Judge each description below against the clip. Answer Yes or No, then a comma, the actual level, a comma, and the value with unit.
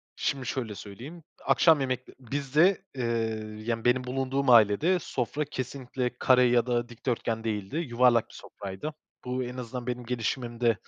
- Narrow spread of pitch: Yes, narrow, 2.3 semitones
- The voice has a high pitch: No, low, 125 Hz